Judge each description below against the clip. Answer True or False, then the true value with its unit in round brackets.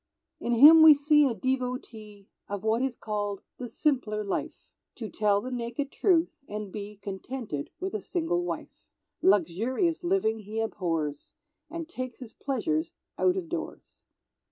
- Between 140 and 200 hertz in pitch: False (245 Hz)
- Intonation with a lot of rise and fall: True (6.8 semitones)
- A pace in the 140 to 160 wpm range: True (150 wpm)